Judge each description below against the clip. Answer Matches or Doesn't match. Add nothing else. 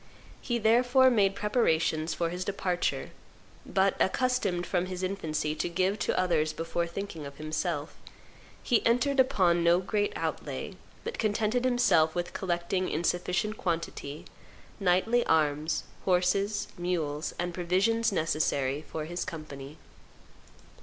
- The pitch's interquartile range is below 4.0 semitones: Doesn't match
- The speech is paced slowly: Matches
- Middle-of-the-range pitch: Matches